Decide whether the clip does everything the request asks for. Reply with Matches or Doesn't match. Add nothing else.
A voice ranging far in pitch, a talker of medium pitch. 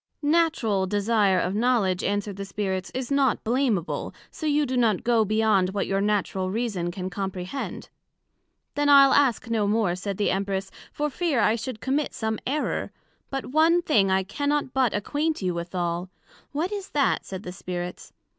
Doesn't match